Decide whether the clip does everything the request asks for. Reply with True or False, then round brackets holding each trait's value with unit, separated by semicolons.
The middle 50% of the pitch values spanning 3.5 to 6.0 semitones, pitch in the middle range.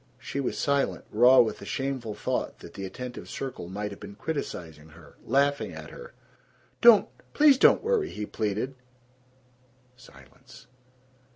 False (5.5 semitones; 125 Hz)